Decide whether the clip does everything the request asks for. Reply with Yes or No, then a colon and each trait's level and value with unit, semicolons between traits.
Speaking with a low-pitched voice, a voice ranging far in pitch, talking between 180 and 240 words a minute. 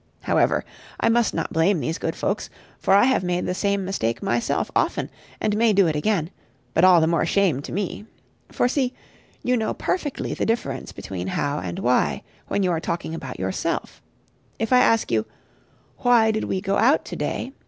No: high, 190 Hz; wide, 5.8 semitones; average, 195 wpm